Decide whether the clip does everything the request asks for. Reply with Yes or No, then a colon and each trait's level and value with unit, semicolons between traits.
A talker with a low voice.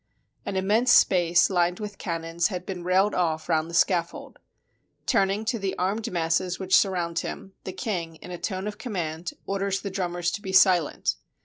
No: medium, 185 Hz